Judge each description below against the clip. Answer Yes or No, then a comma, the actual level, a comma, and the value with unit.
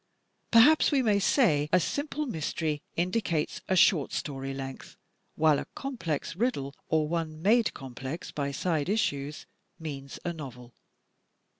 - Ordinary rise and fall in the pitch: No, wide, 6.5 semitones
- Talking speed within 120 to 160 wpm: Yes, slow, 135 wpm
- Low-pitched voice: No, medium, 160 Hz